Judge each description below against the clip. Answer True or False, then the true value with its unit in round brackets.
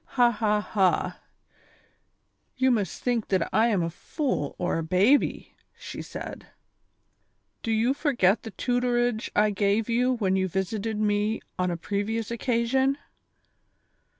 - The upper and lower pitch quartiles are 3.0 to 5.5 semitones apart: True (3.7 semitones)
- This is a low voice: False (220 Hz)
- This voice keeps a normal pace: True (145 wpm)